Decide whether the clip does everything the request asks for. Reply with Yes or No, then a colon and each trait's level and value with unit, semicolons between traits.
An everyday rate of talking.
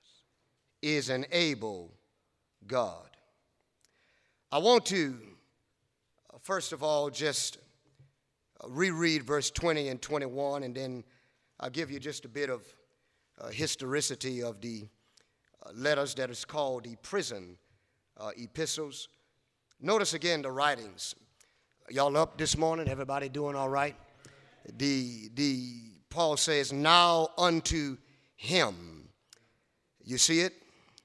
No: slow, 120 wpm